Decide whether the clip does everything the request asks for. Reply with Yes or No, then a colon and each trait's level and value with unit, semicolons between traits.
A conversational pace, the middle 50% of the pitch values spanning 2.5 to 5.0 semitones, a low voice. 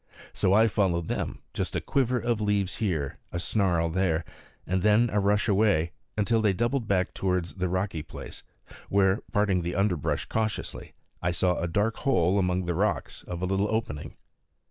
Yes: average, 175 wpm; average, 3.2 semitones; very low, 95 Hz